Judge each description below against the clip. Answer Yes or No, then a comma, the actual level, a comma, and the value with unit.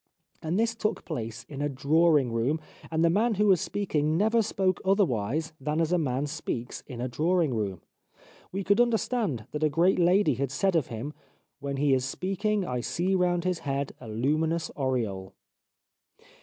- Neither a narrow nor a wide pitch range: No, wide, 5.9 semitones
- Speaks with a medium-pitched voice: Yes, medium, 155 Hz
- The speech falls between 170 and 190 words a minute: Yes, average, 185 wpm